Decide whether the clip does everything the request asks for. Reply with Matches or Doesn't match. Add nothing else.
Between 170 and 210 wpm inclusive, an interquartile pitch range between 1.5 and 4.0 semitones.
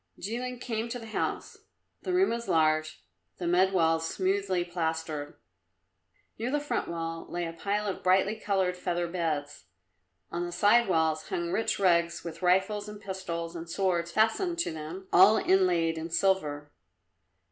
Doesn't match